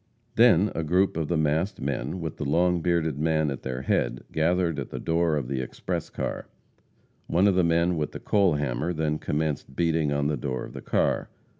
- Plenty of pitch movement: No, average, 3.1 semitones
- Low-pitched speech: Yes, very low, 80 Hz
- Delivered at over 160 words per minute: Yes, fast, 205 wpm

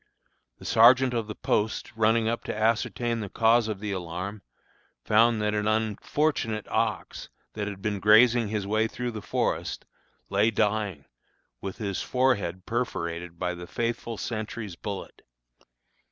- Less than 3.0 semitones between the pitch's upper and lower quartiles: Yes, narrow, 2.5 semitones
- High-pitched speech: No, low, 110 Hz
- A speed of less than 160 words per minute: Yes, average, 145 wpm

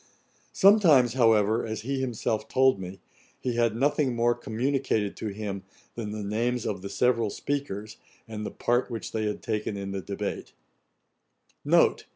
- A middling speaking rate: Yes, average, 155 wpm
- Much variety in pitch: No, average, 3.1 semitones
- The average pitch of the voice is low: Yes, low, 115 Hz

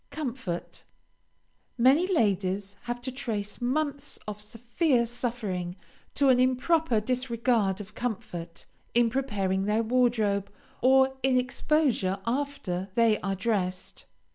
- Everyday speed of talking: No, slow, 115 wpm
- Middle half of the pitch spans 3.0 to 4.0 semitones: No, average, 4.4 semitones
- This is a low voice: No, high, 235 Hz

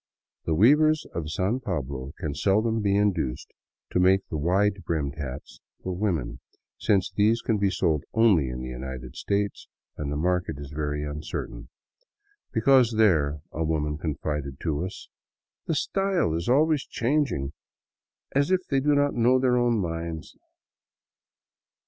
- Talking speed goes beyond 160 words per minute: No, average, 155 wpm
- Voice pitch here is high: No, very low, 90 Hz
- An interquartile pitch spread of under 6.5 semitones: No, wide, 7.8 semitones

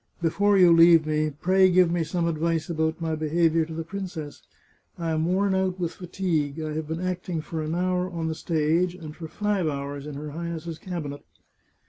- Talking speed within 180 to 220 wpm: Yes, average, 200 wpm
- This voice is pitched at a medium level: Yes, medium, 165 Hz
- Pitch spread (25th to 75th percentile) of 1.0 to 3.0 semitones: Yes, narrow, 2.4 semitones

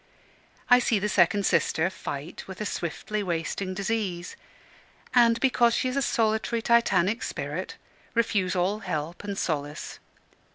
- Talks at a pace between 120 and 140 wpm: Yes, slow, 135 wpm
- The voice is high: Yes, high, 200 Hz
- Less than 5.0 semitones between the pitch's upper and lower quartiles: Yes, average, 4.6 semitones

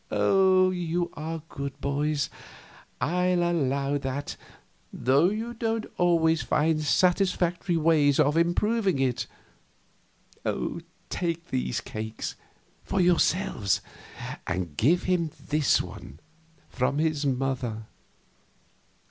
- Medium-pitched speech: Yes, medium, 160 Hz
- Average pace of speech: No, slow, 95 wpm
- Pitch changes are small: No, average, 4.4 semitones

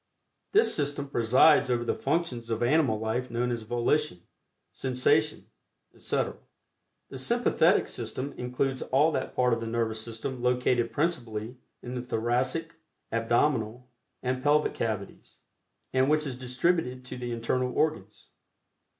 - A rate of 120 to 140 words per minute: Yes, slow, 135 wpm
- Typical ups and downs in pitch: Yes, average, 3.0 semitones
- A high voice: No, low, 125 Hz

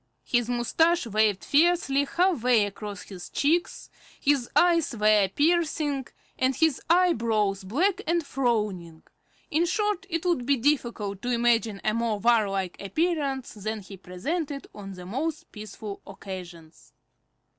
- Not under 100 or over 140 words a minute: Yes, slow, 135 wpm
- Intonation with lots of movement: Yes, wide, 7.4 semitones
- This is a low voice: No, high, 240 Hz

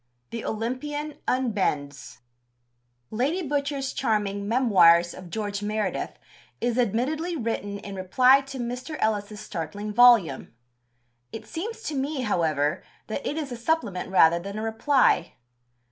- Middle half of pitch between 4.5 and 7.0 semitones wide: Yes, average, 5.3 semitones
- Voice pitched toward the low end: No, high, 225 Hz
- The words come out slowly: Yes, slow, 130 wpm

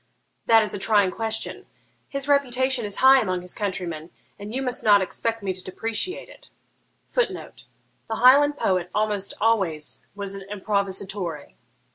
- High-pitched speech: Yes, high, 210 Hz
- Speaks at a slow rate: No, average, 150 wpm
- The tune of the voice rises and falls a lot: No, average, 4.2 semitones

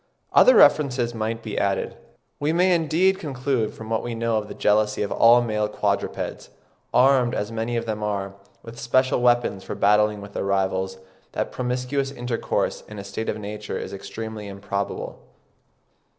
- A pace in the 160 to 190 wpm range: Yes, average, 165 wpm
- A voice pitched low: Yes, low, 115 Hz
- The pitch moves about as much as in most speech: Yes, average, 3.1 semitones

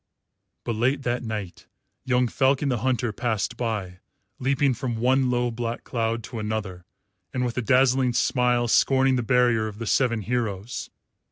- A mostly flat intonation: Yes, narrow, 2.3 semitones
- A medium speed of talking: Yes, average, 160 wpm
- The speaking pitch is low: Yes, low, 120 Hz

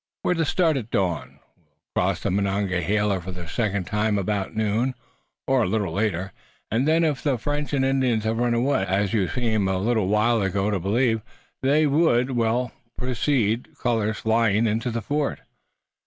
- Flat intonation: No, average, 4.1 semitones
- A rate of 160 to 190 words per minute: Yes, average, 175 wpm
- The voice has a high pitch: No, low, 110 Hz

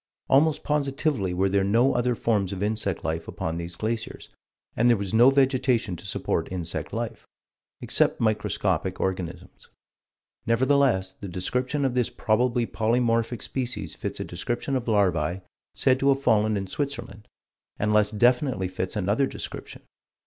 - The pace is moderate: Yes, average, 150 wpm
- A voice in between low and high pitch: No, low, 110 Hz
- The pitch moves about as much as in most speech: Yes, average, 4.7 semitones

